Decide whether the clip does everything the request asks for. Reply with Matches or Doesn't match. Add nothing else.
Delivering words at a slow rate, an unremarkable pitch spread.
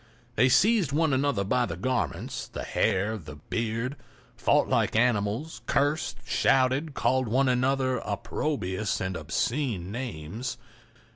Matches